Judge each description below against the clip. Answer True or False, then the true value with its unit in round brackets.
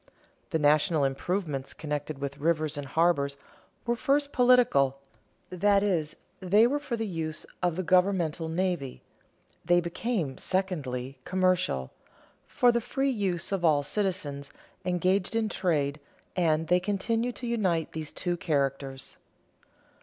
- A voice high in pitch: False (175 Hz)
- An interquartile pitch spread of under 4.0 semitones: False (5.0 semitones)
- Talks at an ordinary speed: False (130 wpm)